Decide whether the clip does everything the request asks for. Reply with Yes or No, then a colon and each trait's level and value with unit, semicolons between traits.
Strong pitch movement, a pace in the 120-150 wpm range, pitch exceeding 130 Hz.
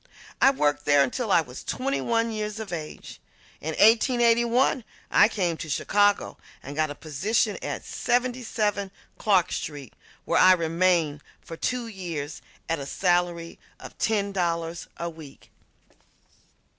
Yes: wide, 5.8 semitones; average, 140 wpm; medium, 185 Hz